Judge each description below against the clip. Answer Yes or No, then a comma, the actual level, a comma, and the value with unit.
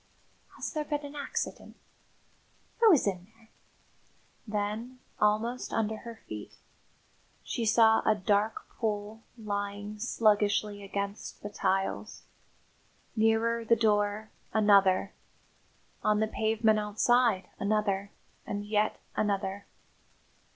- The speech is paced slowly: Yes, slow, 105 wpm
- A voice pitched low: No, high, 215 Hz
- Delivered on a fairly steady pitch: Yes, narrow, 1.6 semitones